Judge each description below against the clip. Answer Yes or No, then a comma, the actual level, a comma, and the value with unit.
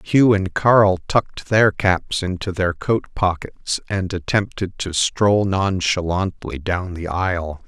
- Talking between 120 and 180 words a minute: Yes, average, 140 wpm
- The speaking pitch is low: Yes, very low, 95 Hz